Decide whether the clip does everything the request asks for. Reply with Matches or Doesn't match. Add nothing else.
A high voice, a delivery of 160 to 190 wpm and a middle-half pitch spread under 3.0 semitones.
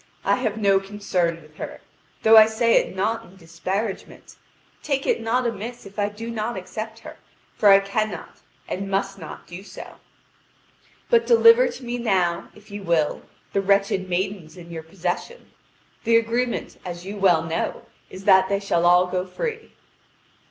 Doesn't match